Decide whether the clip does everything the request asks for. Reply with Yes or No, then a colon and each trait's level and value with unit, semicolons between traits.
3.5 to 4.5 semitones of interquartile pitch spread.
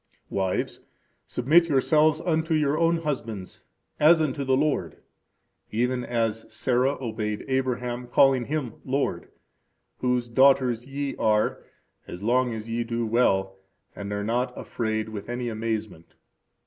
Yes: average, 3.8 semitones